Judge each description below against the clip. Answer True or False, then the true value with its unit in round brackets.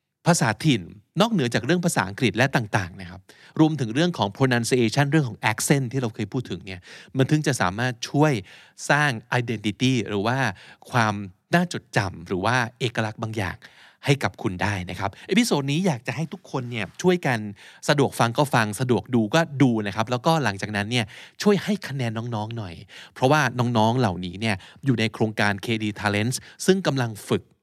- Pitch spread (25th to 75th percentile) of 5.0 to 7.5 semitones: True (5.3 semitones)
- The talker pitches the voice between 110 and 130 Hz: True (125 Hz)